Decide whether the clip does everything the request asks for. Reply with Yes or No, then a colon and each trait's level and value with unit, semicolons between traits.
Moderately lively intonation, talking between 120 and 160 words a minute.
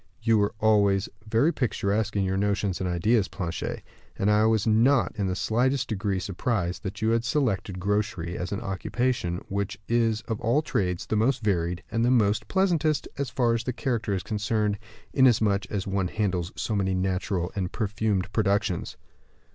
No: average, 3.1 semitones; average, 180 wpm